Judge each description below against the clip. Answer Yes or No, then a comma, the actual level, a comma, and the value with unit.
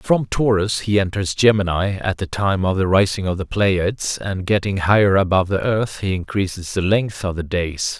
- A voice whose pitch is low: Yes, very low, 95 Hz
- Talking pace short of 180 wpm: No, fast, 205 wpm